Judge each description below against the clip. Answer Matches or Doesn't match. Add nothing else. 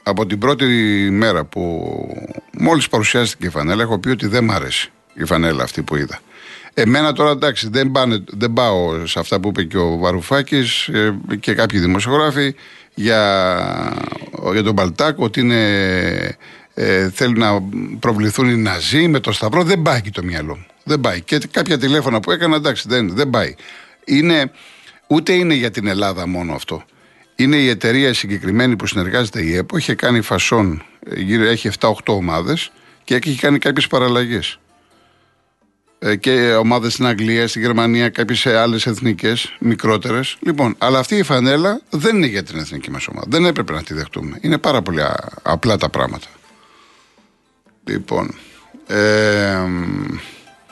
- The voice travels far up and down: Doesn't match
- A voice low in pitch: Matches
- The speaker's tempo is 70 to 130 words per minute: Doesn't match